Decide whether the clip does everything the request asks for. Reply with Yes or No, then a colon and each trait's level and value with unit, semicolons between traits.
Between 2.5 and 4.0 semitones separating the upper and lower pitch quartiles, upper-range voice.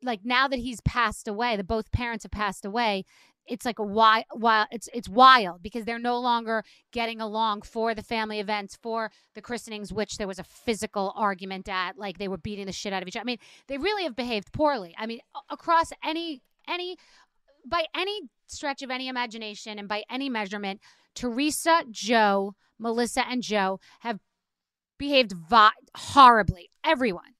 Yes: average, 3.3 semitones; high, 230 Hz